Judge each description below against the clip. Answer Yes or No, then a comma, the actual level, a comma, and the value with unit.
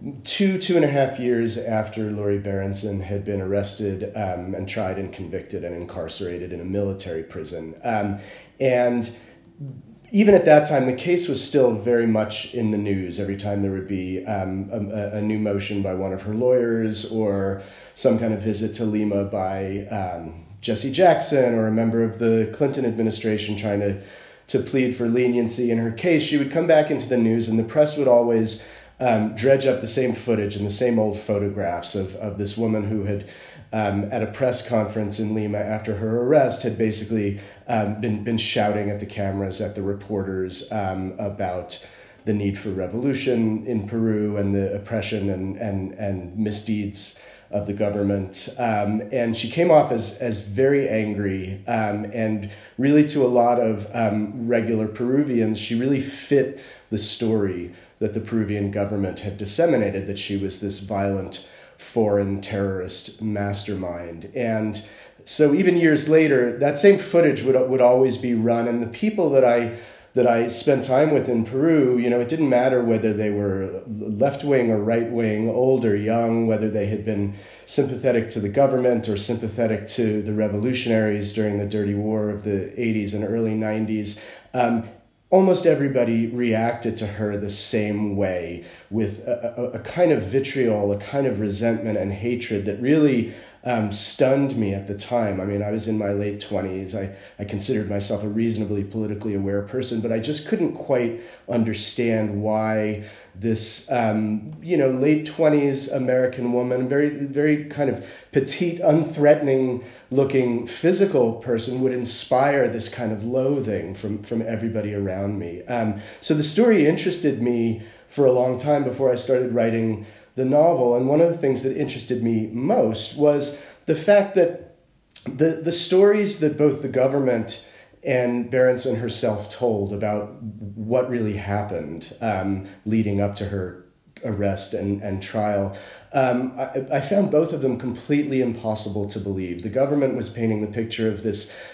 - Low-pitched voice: Yes, low, 110 Hz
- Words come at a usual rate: Yes, average, 170 wpm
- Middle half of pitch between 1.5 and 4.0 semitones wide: Yes, average, 3.7 semitones